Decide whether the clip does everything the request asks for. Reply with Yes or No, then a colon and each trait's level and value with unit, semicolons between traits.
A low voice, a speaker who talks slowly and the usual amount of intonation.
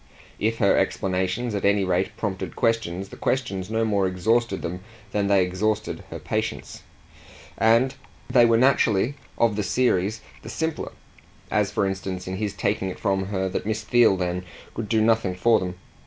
No: low, 105 Hz; average, 170 wpm; average, 3.2 semitones